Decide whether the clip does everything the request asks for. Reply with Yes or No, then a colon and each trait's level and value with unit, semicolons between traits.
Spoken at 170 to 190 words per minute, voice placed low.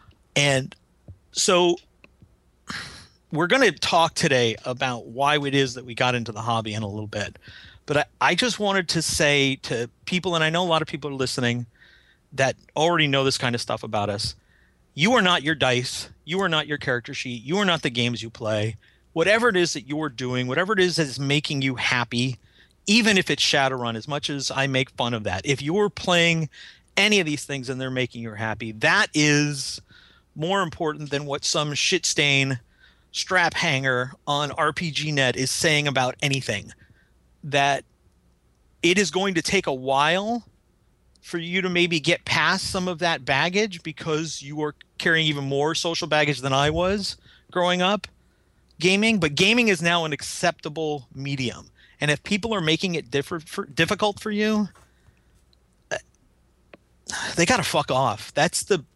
No: average, 180 wpm; medium, 145 Hz